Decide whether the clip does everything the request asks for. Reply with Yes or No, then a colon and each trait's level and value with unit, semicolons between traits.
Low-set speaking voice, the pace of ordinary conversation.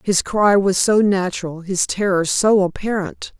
No: high, 190 Hz; average, 160 wpm